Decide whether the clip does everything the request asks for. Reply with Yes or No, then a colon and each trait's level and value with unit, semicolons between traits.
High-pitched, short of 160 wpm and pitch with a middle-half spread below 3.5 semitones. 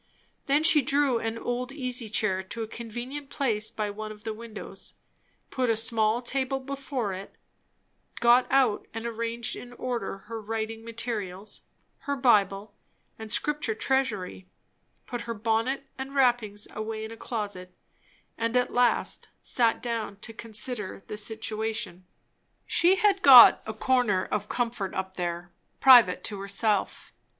Yes: high, 225 Hz; average, 145 wpm; average, 3.0 semitones